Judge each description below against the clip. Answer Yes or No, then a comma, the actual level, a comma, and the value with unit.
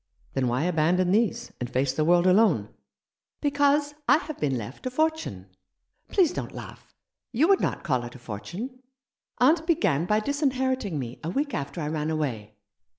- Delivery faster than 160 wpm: Yes, average, 170 wpm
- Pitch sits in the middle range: Yes, medium, 180 Hz